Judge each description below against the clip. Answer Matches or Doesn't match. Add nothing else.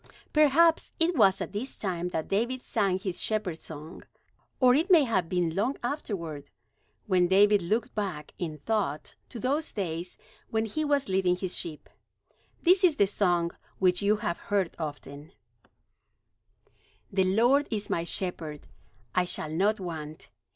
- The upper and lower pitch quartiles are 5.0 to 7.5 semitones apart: Matches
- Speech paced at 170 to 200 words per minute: Doesn't match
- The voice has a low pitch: Doesn't match